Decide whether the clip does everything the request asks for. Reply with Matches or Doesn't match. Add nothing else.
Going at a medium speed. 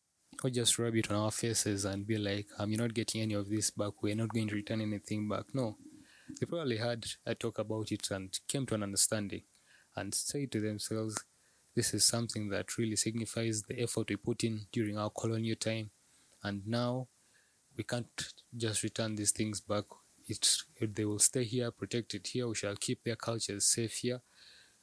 Matches